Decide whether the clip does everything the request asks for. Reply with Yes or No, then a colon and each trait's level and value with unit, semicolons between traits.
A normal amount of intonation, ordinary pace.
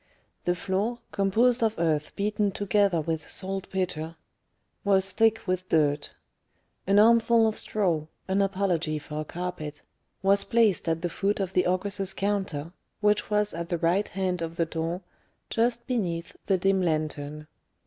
Yes: average, 3.6 semitones; average, 150 wpm